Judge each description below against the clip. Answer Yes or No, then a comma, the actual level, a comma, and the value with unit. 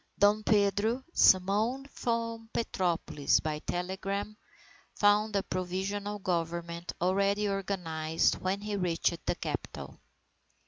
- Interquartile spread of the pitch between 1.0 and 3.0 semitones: Yes, average, 2.7 semitones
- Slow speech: Yes, slow, 100 wpm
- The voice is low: No, high, 195 Hz